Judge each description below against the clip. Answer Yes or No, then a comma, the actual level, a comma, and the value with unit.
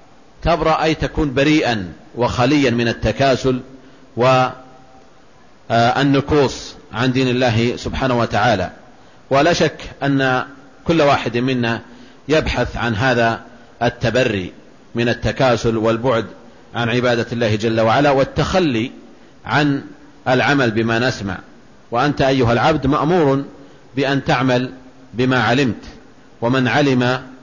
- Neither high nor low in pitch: No, low, 130 Hz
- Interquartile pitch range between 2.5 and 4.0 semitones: Yes, average, 2.8 semitones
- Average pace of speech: Yes, average, 100 wpm